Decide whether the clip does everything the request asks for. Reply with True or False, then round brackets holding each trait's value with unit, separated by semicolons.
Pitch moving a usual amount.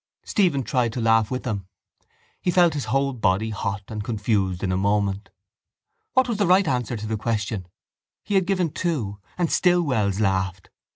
False (8.0 semitones)